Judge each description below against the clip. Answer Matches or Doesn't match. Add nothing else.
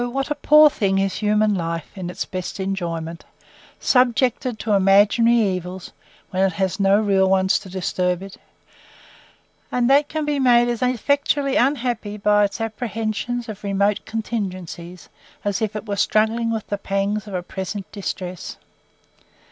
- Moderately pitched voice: Doesn't match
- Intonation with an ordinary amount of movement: Matches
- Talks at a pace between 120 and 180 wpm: Matches